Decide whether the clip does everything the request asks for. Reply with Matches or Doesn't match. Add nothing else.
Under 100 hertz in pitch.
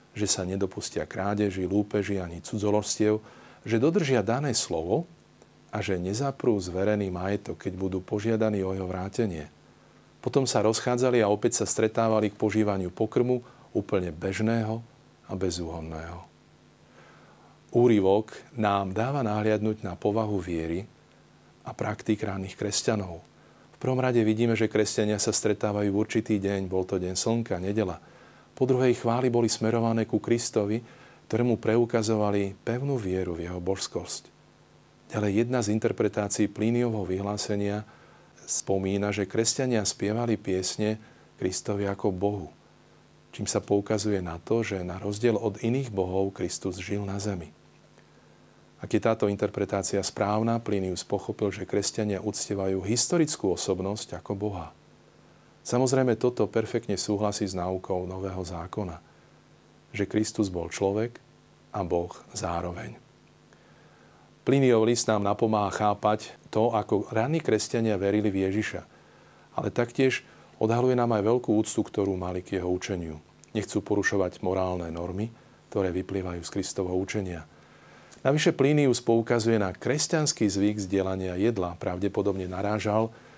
Doesn't match